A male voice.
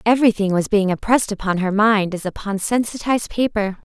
No: female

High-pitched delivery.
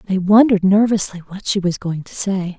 Yes: high, 195 Hz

